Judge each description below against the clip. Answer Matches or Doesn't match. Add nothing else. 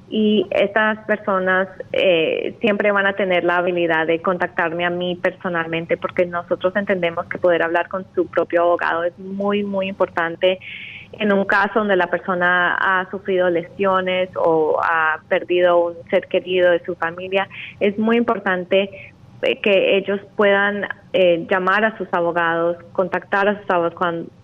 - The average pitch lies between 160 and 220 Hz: Matches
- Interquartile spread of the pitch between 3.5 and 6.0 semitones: Doesn't match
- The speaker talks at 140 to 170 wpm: Matches